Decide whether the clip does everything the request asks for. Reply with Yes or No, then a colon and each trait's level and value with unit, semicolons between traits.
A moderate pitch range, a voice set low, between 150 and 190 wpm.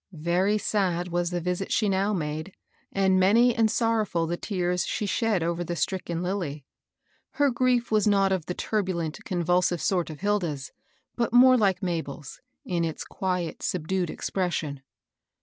No: average, 3.3 semitones; medium, 180 Hz; average, 160 wpm